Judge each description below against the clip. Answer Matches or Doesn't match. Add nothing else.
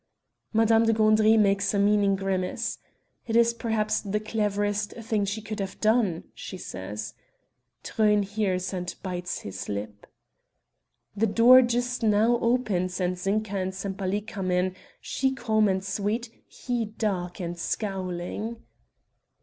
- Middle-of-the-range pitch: Doesn't match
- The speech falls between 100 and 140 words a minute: Matches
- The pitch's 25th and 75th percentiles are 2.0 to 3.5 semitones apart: Matches